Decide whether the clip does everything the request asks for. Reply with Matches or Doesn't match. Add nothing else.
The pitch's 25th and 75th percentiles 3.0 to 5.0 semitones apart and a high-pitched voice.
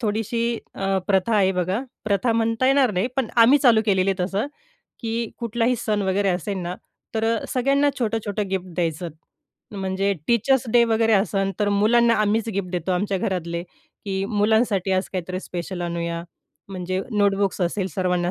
Matches